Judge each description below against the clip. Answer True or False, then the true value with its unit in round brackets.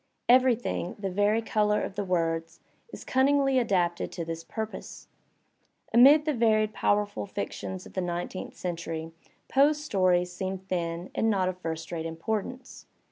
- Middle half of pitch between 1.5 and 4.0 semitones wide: False (4.4 semitones)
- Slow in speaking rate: False (150 wpm)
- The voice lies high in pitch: True (195 Hz)